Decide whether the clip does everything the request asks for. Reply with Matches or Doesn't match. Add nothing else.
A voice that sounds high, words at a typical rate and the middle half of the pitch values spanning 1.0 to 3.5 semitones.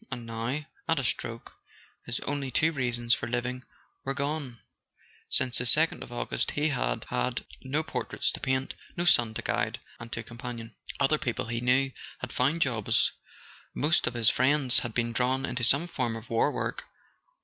Doesn't match